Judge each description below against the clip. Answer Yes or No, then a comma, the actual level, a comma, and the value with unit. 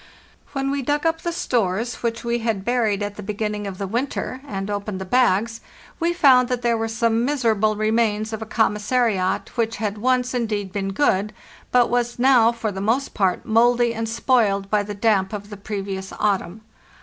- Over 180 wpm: Yes, average, 190 wpm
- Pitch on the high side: Yes, high, 225 Hz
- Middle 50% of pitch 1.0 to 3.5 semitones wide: Yes, average, 3.0 semitones